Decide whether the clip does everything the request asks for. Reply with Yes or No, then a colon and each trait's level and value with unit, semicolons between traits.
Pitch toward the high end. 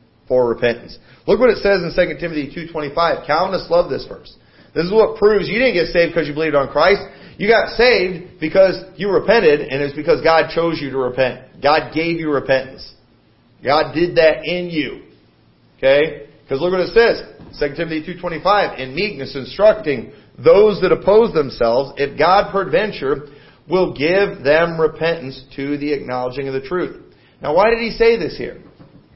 No: medium, 160 Hz